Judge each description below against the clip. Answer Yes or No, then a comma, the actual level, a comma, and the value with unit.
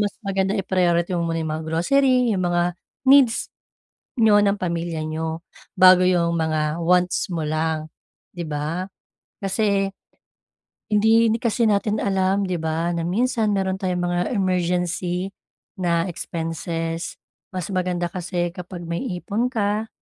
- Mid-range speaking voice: Yes, medium, 180 Hz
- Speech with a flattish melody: No, average, 3.0 semitones